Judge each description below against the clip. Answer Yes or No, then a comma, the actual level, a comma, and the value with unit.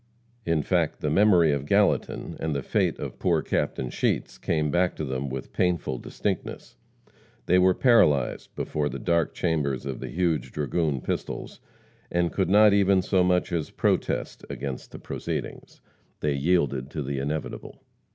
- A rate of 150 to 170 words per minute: Yes, average, 160 wpm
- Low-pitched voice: Yes, very low, 80 Hz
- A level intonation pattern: No, average, 4.4 semitones